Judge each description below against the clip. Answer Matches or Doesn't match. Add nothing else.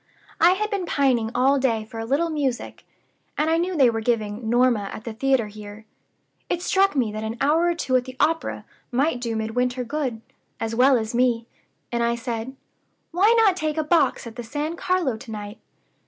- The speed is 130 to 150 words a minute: Doesn't match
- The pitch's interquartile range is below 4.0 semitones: Doesn't match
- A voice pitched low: Doesn't match